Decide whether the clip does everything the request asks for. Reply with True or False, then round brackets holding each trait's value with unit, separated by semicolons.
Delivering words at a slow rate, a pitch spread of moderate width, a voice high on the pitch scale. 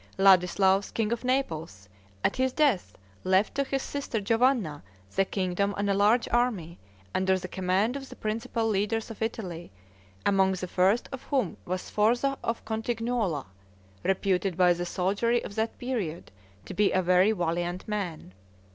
False (155 wpm; 4.1 semitones; 200 Hz)